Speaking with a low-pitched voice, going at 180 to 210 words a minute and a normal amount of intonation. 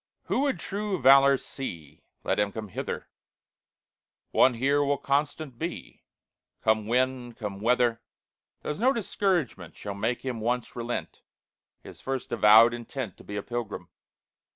No: low, 125 Hz; average, 140 wpm; average, 4.1 semitones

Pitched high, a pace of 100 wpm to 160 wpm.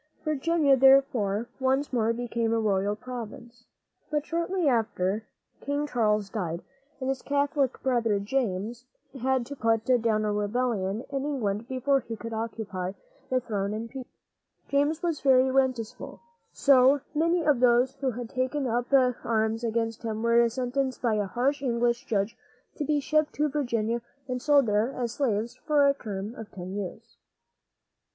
Yes: high, 240 Hz; average, 155 wpm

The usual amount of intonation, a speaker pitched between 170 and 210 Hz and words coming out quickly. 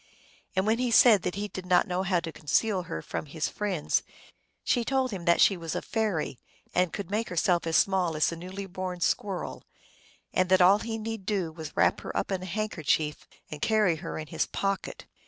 Yes: average, 3.6 semitones; medium, 185 Hz; fast, 215 wpm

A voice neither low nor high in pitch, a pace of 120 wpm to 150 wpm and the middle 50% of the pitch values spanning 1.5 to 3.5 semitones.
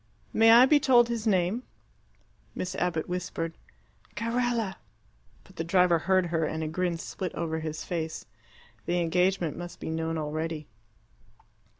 Yes: medium, 175 Hz; average, 140 wpm; average, 3.2 semitones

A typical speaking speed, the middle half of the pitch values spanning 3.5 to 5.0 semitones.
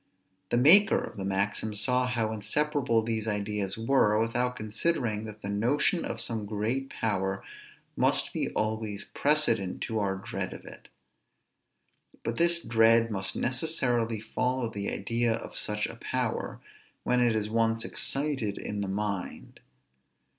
No: average, 145 wpm; average, 3.1 semitones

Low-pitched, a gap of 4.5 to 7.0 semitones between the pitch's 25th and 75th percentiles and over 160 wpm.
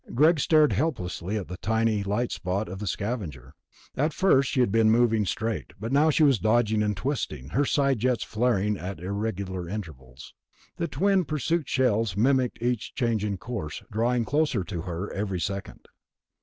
Yes: low, 110 Hz; average, 4.9 semitones; average, 170 wpm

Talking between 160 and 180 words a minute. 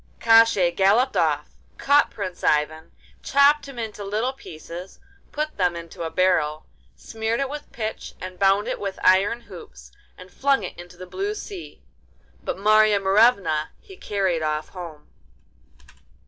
No: average, 150 wpm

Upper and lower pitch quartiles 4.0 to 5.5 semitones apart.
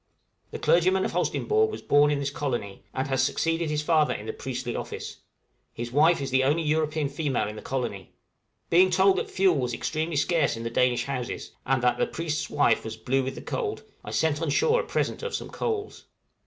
Yes: average, 4.3 semitones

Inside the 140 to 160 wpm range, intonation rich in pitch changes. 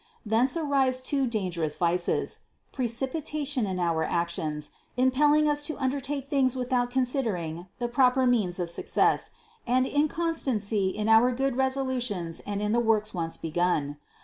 Yes: average, 145 wpm; wide, 6.6 semitones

